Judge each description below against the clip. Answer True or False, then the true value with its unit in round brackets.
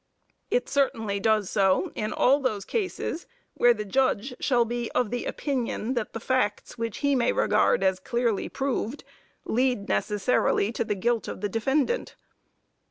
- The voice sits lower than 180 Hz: False (235 Hz)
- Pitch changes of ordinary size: True (3.9 semitones)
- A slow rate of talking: False (160 wpm)